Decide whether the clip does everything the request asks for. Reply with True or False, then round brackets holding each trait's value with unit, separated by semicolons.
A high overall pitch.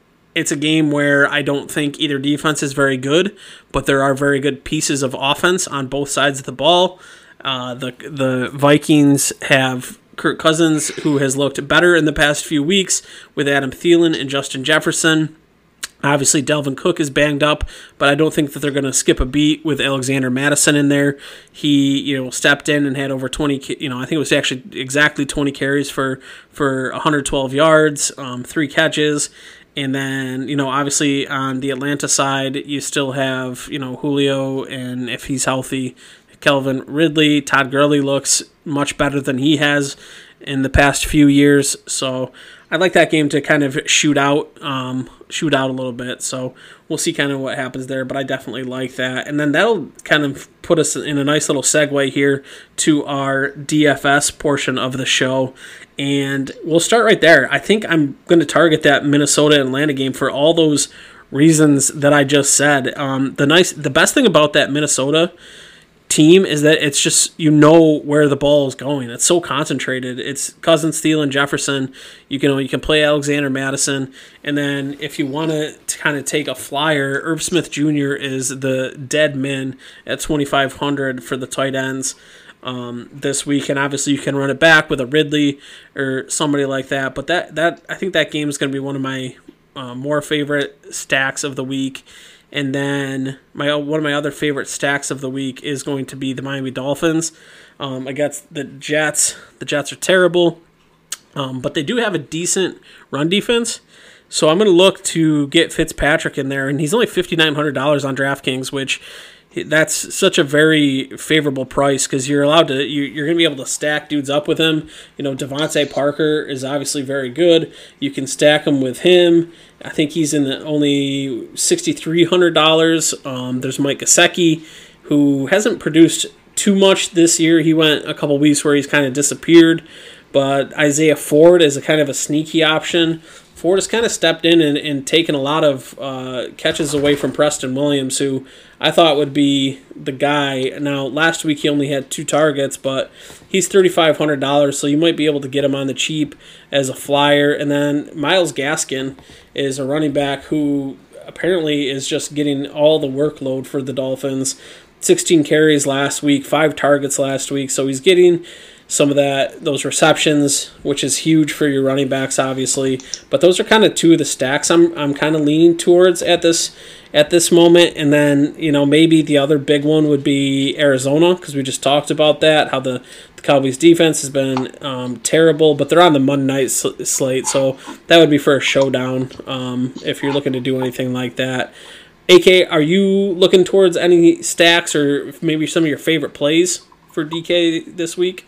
False (145 Hz)